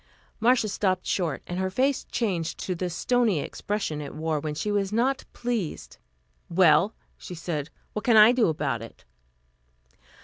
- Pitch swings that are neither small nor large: No, wide, 5.8 semitones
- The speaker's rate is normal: Yes, average, 160 wpm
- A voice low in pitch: No, high, 190 Hz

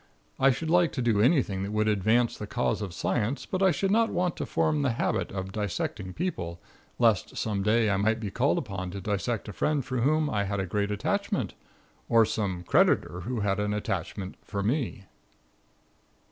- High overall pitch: No, low, 110 Hz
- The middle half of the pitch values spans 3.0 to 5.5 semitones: Yes, average, 4.7 semitones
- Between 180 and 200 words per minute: Yes, average, 195 wpm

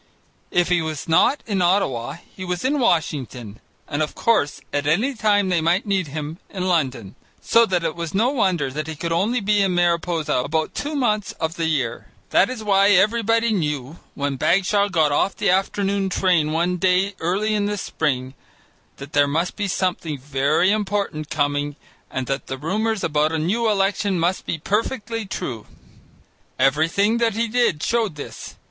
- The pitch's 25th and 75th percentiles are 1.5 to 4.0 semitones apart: No, average, 5.2 semitones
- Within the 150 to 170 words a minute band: No, average, 180 wpm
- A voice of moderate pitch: Yes, medium, 180 Hz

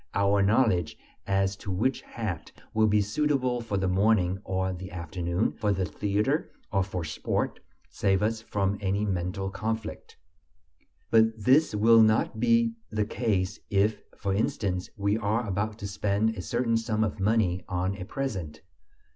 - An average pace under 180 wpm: Yes, average, 155 wpm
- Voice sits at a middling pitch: No, low, 100 Hz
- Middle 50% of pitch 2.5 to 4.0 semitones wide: Yes, average, 2.9 semitones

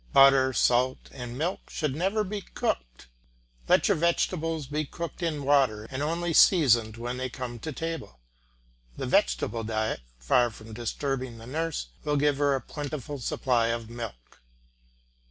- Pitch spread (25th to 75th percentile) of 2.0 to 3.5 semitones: No, average, 4.7 semitones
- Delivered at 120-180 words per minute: Yes, average, 155 wpm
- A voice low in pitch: Yes, low, 130 Hz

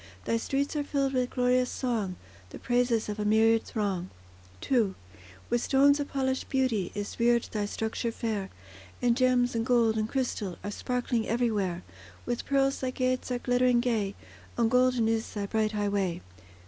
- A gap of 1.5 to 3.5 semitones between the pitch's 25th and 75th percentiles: Yes, average, 2.9 semitones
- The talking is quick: No, average, 165 wpm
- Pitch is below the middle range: No, high, 235 Hz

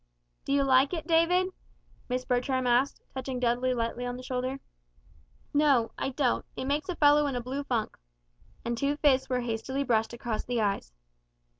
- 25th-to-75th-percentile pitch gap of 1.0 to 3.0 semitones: Yes, narrow, 2.5 semitones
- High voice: Yes, very high, 255 Hz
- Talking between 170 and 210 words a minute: Yes, average, 175 wpm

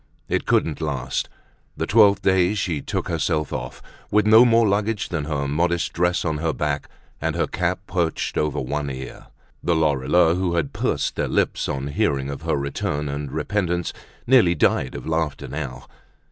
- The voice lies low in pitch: Yes, very low, 80 Hz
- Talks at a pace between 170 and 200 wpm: Yes, average, 175 wpm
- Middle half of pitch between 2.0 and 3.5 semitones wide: No, average, 4.2 semitones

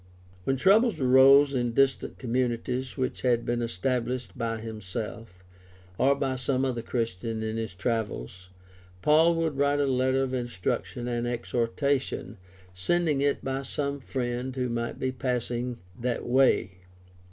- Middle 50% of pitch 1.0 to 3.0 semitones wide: Yes, narrow, 2.5 semitones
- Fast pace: No, average, 140 wpm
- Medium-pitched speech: No, low, 125 Hz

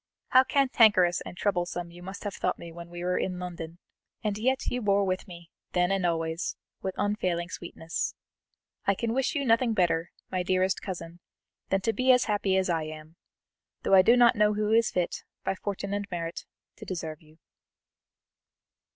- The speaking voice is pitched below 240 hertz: Yes, medium, 185 Hz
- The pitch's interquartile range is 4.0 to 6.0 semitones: No, average, 3.4 semitones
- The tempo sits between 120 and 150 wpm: No, average, 185 wpm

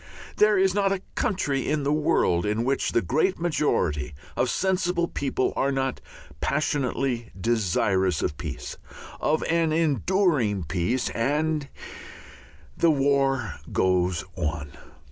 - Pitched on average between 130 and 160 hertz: Yes, low, 135 Hz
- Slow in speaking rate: Yes, slow, 125 wpm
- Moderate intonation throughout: No, wide, 8.6 semitones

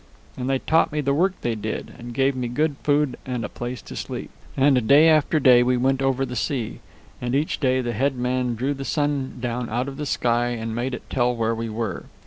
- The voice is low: Yes, low, 125 Hz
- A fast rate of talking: Yes, fast, 235 wpm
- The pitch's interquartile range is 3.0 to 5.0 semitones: No, narrow, 2.4 semitones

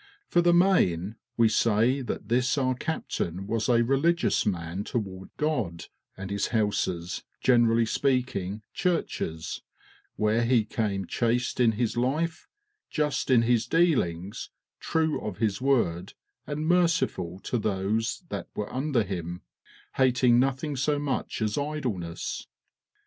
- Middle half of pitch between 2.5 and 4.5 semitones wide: No, wide, 5.5 semitones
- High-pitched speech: No, low, 120 Hz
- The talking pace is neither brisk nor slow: No, slow, 130 wpm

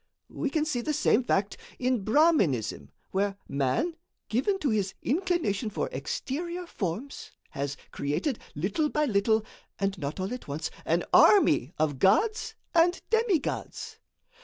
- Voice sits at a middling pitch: No, high, 240 Hz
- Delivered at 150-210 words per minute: No, slow, 135 wpm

